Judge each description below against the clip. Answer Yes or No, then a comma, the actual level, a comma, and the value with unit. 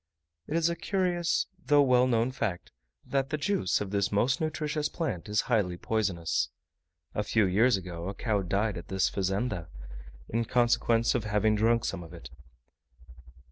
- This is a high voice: No, low, 110 Hz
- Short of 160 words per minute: No, average, 165 wpm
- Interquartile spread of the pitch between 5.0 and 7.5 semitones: Yes, average, 5.3 semitones